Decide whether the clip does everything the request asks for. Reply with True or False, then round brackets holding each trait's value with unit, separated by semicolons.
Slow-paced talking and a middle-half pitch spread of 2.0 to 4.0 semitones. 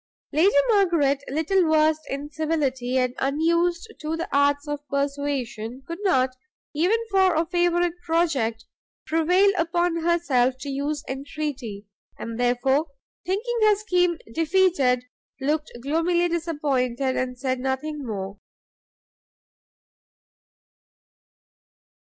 False (105 wpm; 4.4 semitones)